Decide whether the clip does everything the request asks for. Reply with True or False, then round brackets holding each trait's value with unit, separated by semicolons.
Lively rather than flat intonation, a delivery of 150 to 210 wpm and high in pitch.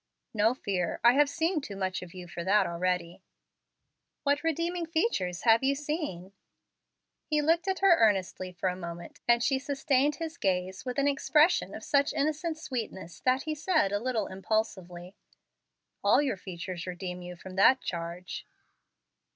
True (8.2 semitones; 160 wpm; 225 Hz)